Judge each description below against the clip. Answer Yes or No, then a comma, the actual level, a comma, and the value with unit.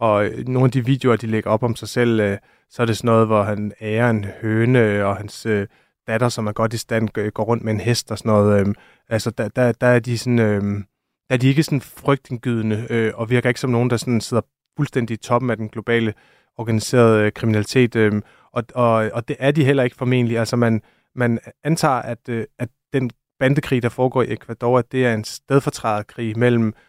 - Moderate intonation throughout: No, narrow, 2.3 semitones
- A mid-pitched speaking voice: No, low, 115 Hz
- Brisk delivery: No, average, 210 wpm